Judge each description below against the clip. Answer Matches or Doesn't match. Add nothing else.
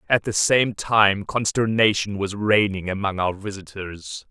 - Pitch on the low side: Matches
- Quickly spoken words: Doesn't match